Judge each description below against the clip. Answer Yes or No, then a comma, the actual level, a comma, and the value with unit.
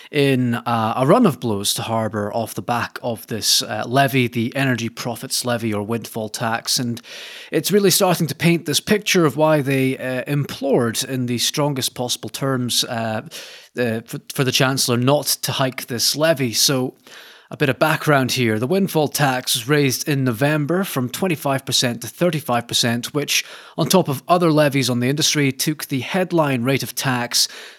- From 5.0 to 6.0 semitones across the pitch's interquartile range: No, average, 3.9 semitones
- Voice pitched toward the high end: No, low, 130 Hz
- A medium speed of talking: Yes, average, 180 wpm